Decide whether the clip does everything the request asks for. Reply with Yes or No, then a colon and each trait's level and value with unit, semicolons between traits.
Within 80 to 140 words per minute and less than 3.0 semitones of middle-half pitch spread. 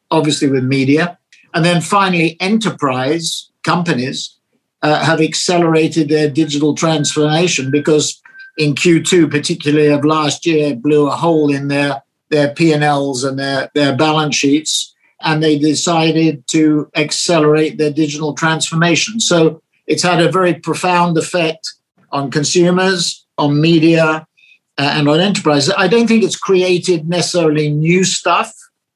Yes: slow, 135 wpm; narrow, 2.5 semitones